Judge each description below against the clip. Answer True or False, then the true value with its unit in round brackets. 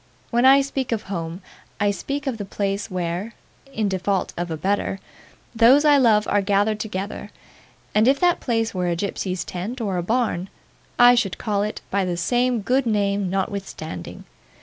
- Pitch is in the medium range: False (205 Hz)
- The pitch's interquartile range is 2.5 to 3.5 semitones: False (4.1 semitones)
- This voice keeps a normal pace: True (175 wpm)